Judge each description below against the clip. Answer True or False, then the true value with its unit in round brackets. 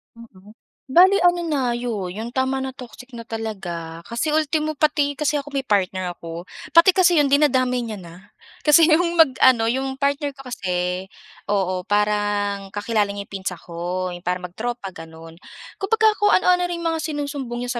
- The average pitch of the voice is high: True (240 Hz)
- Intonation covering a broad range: True (7.4 semitones)